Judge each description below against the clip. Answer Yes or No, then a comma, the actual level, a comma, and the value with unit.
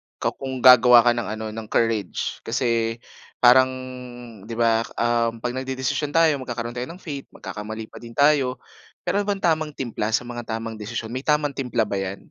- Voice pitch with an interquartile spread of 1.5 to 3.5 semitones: Yes, average, 2.8 semitones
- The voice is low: Yes, low, 120 Hz